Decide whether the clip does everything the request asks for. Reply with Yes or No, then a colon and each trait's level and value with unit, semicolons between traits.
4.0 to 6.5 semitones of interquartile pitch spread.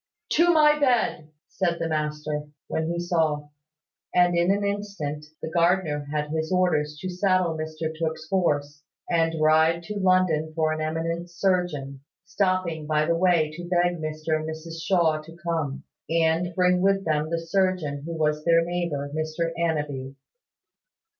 No: narrow, 2.4 semitones